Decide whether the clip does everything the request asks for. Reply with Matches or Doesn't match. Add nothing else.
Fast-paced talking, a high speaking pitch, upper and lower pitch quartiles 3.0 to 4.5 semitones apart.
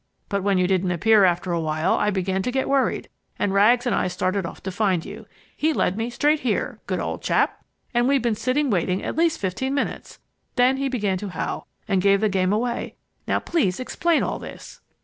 Doesn't match